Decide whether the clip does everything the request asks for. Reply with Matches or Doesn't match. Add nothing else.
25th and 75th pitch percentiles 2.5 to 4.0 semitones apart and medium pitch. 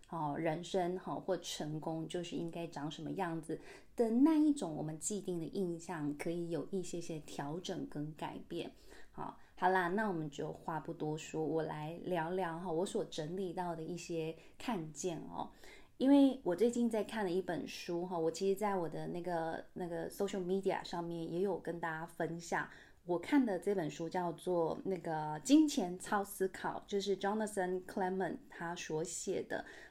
Matches